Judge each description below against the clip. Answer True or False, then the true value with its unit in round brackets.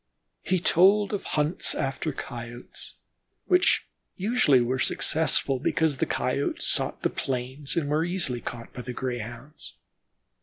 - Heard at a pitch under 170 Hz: True (140 Hz)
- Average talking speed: False (130 wpm)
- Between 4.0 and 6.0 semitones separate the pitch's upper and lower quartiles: True (5.3 semitones)